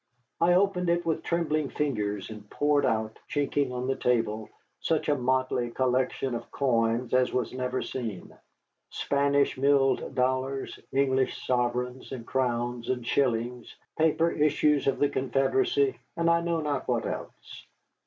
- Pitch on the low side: Yes, low, 130 Hz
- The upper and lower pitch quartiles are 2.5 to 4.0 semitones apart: Yes, average, 3.2 semitones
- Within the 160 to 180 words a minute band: No, average, 145 wpm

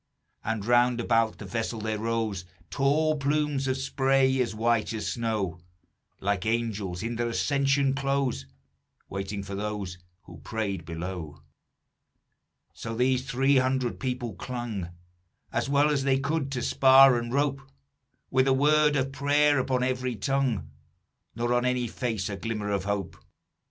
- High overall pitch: No, low, 120 Hz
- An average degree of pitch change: Yes, average, 4.2 semitones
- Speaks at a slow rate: No, average, 145 wpm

